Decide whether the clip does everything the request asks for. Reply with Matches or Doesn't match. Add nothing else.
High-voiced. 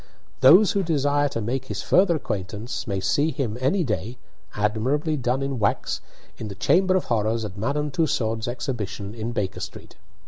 Doesn't match